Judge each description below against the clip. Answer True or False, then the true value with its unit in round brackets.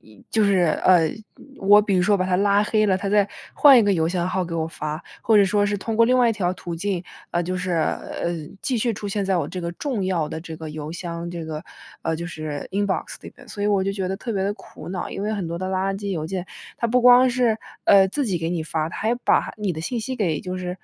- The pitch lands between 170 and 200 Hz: True (190 Hz)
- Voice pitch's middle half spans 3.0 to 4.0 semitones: True (3.3 semitones)